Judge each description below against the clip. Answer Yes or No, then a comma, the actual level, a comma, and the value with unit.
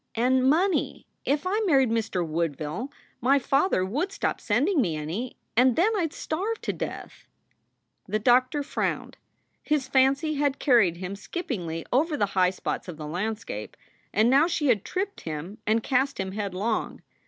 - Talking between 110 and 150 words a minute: No, average, 170 wpm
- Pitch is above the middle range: Yes, high, 245 Hz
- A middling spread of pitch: No, wide, 7.3 semitones